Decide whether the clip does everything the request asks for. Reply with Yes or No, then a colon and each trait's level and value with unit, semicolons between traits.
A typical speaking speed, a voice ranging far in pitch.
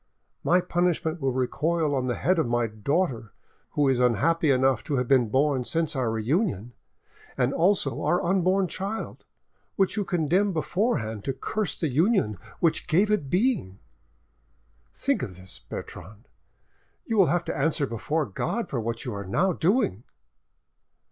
Yes: average, 160 wpm; wide, 6.8 semitones